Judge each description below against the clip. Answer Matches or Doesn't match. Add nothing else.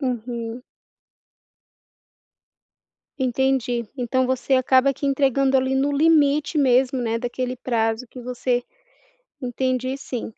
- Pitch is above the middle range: Matches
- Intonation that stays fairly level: Matches